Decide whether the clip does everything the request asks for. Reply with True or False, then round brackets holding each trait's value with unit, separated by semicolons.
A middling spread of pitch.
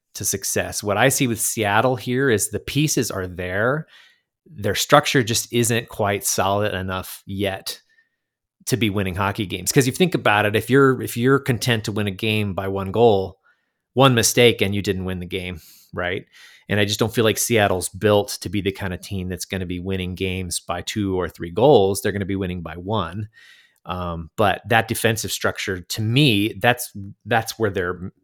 True (3.6 semitones)